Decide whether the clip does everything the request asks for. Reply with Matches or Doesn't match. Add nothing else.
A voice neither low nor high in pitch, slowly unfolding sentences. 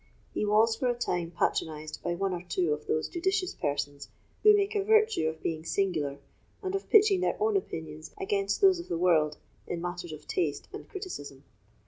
Doesn't match